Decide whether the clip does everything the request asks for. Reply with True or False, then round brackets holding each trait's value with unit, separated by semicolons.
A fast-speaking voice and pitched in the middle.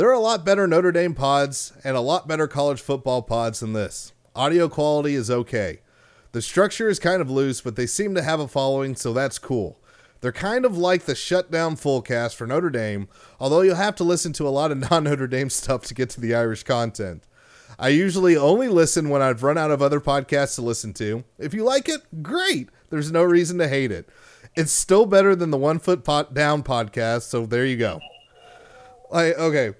True (220 wpm; 145 Hz)